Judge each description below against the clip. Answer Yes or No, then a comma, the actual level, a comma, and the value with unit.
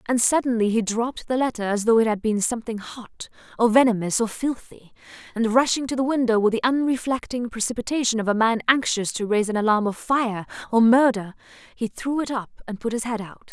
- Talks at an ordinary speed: No, fast, 210 wpm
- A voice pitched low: No, high, 230 Hz